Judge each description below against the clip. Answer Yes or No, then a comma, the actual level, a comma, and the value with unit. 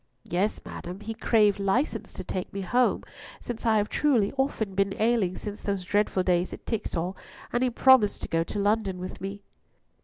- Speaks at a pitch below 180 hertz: No, high, 205 Hz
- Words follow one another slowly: No, average, 190 wpm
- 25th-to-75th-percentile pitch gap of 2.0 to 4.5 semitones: Yes, average, 3.0 semitones